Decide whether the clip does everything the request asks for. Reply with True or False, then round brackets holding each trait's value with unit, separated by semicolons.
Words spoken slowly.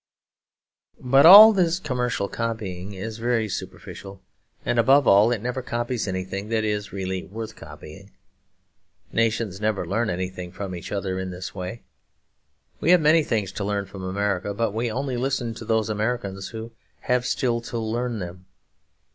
False (160 wpm)